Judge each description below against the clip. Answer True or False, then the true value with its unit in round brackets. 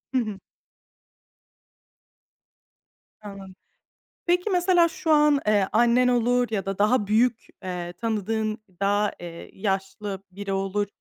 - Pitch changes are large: False (4.1 semitones)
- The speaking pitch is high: True (210 Hz)